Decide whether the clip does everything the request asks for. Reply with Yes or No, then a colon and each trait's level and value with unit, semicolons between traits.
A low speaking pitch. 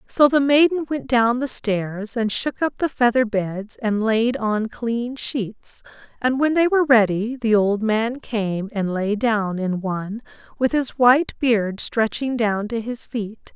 No: high, 230 Hz